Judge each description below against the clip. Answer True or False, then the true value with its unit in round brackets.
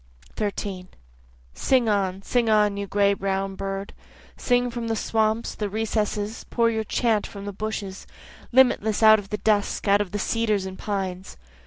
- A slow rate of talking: False (165 wpm)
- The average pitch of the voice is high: True (210 Hz)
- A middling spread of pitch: False (2.0 semitones)